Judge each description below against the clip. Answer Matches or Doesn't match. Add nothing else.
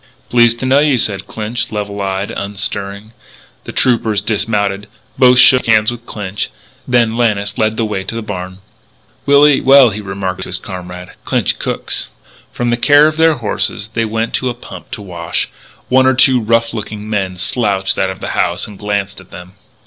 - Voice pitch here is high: Doesn't match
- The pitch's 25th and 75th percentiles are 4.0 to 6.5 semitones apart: Doesn't match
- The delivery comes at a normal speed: Matches